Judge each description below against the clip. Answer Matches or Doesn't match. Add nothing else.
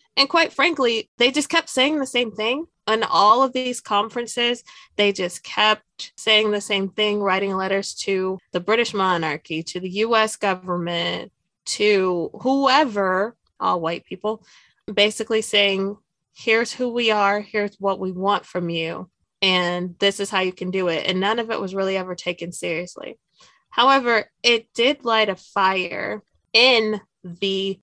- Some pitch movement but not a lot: Matches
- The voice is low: Doesn't match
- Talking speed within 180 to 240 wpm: Doesn't match